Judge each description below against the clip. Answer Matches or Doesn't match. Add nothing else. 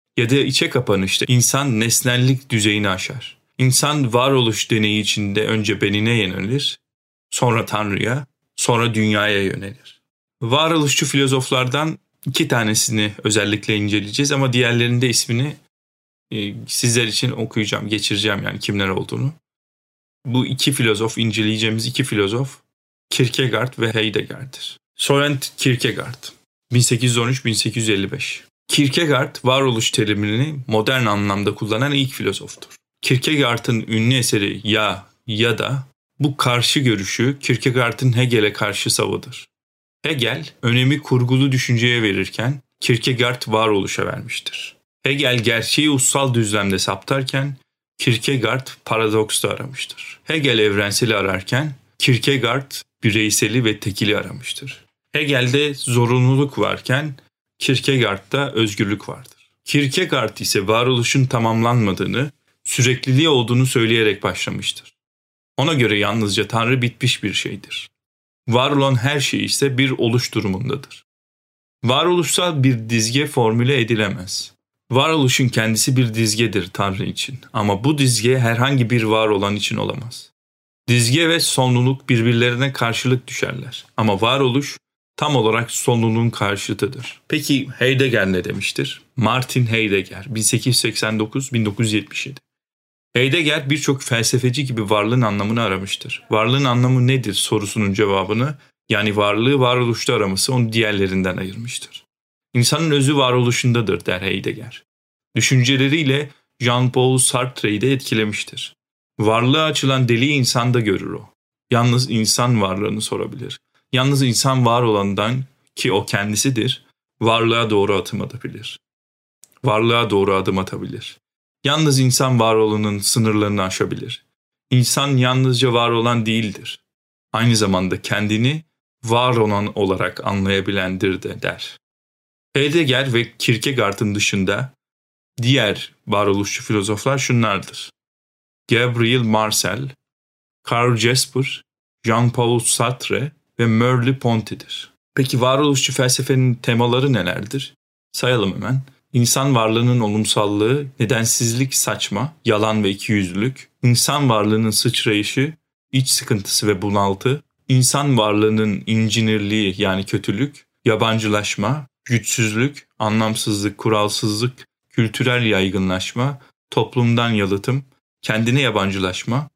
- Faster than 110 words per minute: Doesn't match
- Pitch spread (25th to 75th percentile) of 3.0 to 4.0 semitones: Matches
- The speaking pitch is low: Matches